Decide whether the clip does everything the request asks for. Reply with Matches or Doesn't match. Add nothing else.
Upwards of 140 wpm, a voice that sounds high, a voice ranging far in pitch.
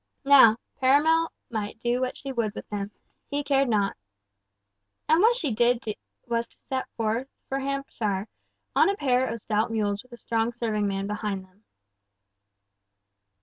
Doesn't match